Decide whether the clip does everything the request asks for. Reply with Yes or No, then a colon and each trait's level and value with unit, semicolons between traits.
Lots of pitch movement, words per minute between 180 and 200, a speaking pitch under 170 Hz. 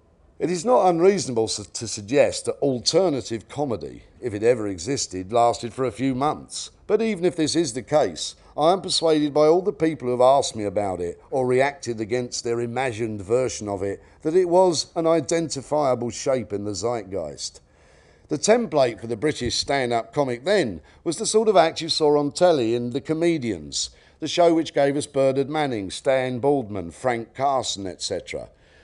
Yes: wide, 6.0 semitones; average, 185 wpm; low, 135 Hz